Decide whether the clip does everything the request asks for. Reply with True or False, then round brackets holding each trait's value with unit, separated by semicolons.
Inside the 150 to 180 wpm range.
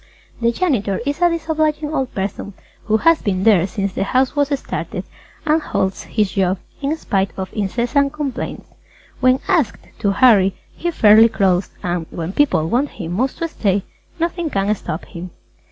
True (170 wpm)